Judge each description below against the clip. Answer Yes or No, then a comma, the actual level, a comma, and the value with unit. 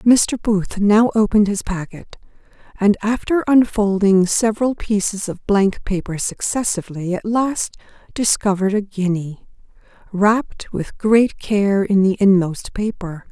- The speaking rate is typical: No, slow, 125 wpm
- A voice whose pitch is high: Yes, high, 205 Hz